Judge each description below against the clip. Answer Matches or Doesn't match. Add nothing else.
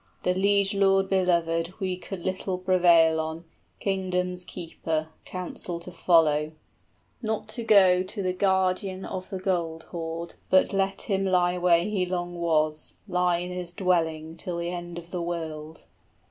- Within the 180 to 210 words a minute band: Doesn't match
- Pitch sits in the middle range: Matches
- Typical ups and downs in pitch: Doesn't match